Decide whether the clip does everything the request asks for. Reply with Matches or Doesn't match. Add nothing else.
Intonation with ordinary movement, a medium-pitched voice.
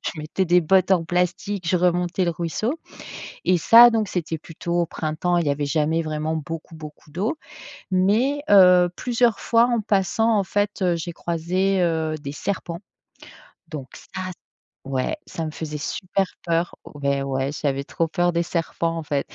Matches